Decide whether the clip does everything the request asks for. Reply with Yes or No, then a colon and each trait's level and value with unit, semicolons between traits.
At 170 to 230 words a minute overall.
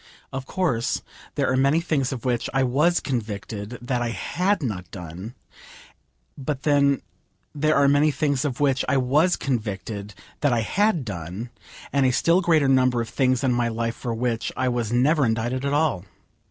Yes: average, 180 wpm